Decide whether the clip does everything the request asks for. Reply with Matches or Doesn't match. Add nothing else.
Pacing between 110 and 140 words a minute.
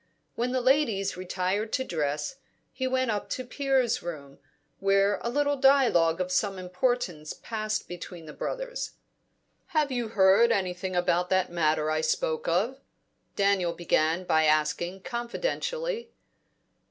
Matches